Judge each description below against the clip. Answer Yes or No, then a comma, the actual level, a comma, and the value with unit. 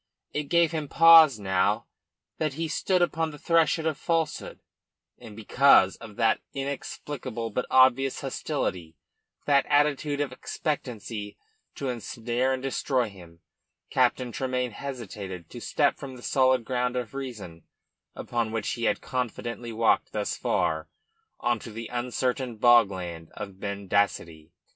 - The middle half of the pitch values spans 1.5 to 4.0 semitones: No, average, 4.5 semitones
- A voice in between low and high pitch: No, low, 125 Hz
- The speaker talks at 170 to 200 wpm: No, slow, 135 wpm